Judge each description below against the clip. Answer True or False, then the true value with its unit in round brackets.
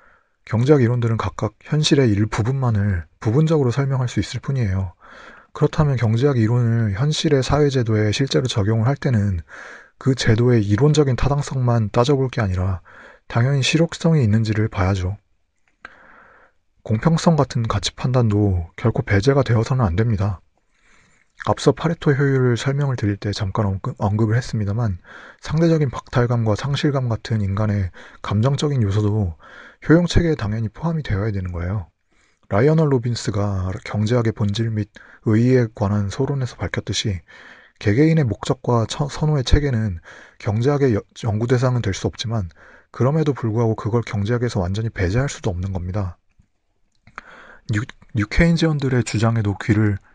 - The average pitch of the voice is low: True (115 Hz)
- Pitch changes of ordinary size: True (4.8 semitones)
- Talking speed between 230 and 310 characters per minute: False (335 characters per minute)